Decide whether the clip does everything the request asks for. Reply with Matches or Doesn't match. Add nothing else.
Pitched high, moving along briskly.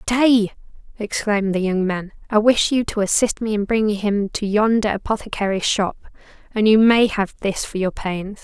Doesn't match